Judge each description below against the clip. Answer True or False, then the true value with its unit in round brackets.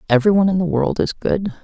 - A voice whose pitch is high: False (170 Hz)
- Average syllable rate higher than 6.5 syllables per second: True (7.3 syllables/s)